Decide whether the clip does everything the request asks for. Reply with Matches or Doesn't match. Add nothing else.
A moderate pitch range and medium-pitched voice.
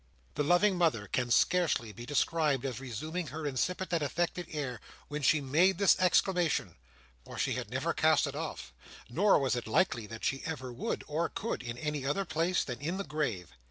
Doesn't match